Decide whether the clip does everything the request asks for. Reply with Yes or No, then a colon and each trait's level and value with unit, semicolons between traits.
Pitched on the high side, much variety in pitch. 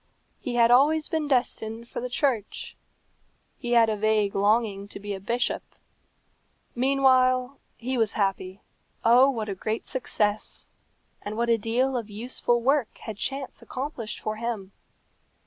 No: high, 235 Hz; average, 3.1 semitones